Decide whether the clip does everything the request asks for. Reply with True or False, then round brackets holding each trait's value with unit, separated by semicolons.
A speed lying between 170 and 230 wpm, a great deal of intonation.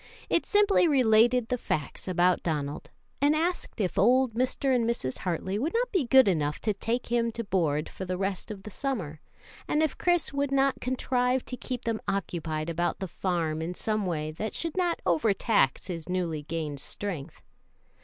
True (185 wpm; 7.2 semitones)